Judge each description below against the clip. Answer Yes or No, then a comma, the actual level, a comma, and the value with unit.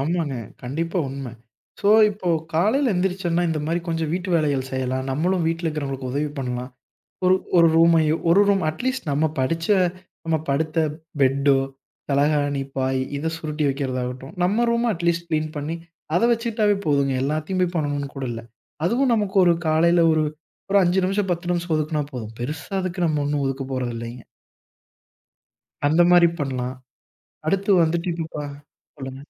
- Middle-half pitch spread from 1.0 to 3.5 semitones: No, average, 4.2 semitones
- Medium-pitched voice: Yes, medium, 155 Hz